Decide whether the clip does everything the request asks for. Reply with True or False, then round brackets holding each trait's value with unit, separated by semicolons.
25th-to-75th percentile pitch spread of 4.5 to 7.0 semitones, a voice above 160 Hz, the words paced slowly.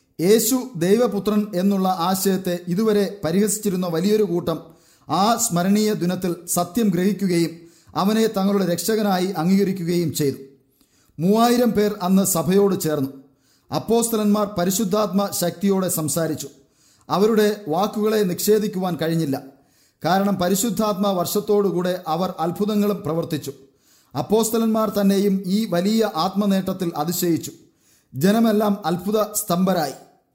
False (4.1 semitones; 190 Hz; 90 wpm)